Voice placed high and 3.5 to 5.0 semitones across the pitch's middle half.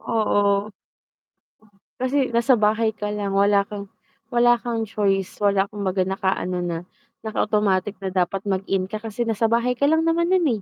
No: high, 210 Hz; average, 3.1 semitones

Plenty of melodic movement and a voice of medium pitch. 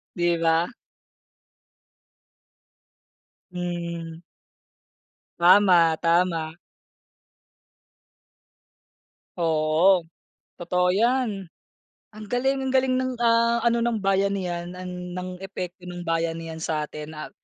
No: average, 3.6 semitones; medium, 180 Hz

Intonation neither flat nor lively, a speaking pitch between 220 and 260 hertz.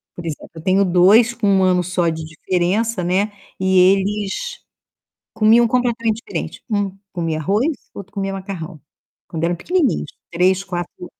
No: average, 3.2 semitones; high, 190 Hz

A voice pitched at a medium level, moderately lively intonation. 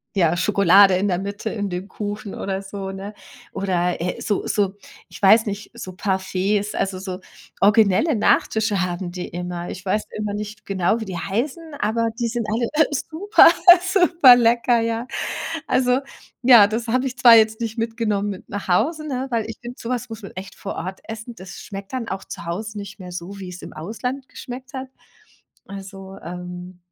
No: high, 205 Hz; average, 3.5 semitones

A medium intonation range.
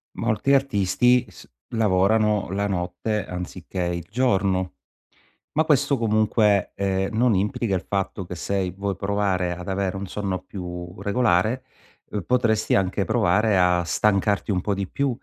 Yes: average, 3.0 semitones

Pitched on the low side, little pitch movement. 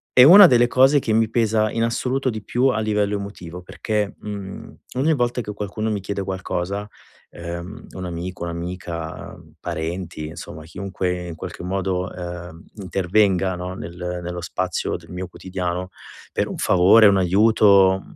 No: very low, 95 Hz; average, 3.4 semitones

